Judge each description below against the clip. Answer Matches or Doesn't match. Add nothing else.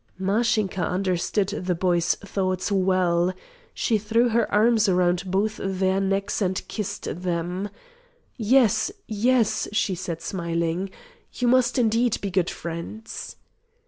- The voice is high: Matches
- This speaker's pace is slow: Matches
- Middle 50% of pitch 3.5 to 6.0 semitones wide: Doesn't match